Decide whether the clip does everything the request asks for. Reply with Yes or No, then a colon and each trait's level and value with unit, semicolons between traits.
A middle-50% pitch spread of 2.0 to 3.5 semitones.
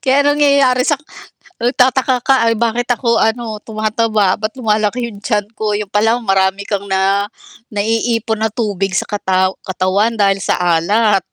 Yes: average, 2.9 semitones